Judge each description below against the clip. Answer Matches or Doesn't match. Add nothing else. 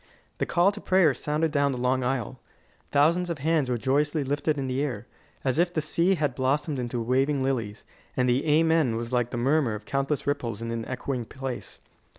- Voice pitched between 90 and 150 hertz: Matches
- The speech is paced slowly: Doesn't match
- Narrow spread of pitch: Doesn't match